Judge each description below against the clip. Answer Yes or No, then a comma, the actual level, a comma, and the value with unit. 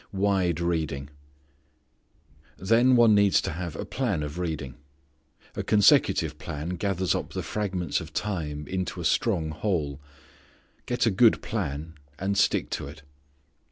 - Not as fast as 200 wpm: Yes, average, 140 wpm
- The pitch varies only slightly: No, average, 4.9 semitones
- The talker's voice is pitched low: Yes, very low, 90 Hz